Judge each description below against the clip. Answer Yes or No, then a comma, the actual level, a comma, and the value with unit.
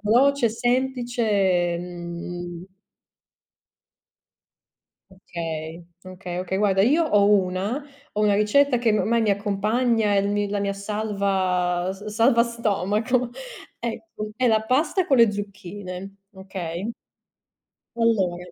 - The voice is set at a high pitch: Yes, high, 205 Hz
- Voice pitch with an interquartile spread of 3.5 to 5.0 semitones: Yes, average, 3.9 semitones